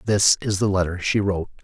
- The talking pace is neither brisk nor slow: No, fast, 220 wpm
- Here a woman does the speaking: No, male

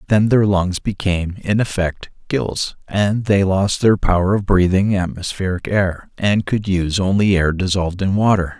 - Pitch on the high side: No, very low, 95 Hz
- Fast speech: No, average, 170 wpm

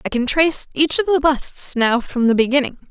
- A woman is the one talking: Yes, female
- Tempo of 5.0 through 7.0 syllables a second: Yes, 5.5 syllables/s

